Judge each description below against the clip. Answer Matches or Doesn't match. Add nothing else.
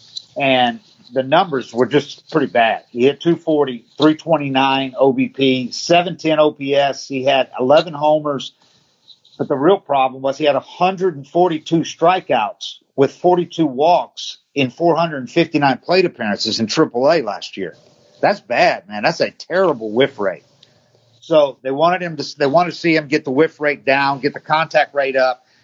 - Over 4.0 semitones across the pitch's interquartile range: Doesn't match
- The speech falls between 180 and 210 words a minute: Doesn't match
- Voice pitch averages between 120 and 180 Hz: Matches